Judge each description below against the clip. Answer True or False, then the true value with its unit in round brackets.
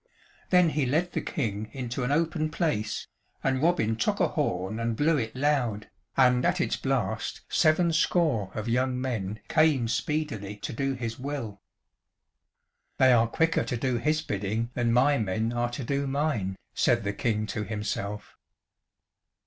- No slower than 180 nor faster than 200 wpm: False (160 wpm)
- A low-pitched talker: True (120 Hz)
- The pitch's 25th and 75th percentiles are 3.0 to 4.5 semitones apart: False (5.0 semitones)